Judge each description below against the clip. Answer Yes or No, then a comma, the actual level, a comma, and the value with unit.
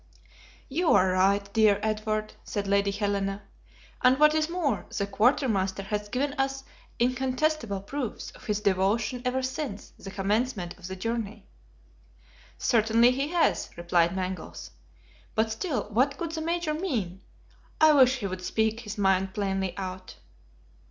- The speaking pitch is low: No, high, 215 Hz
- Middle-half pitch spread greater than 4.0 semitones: Yes, average, 5.1 semitones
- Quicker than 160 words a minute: No, average, 145 wpm